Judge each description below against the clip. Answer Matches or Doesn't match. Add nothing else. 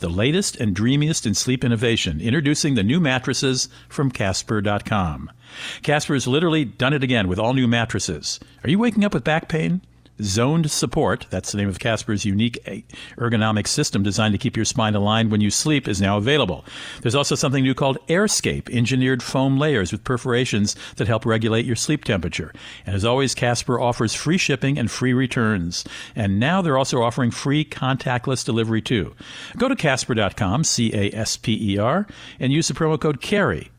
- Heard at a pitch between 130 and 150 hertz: Doesn't match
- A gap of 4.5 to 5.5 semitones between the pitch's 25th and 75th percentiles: Matches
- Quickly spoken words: Doesn't match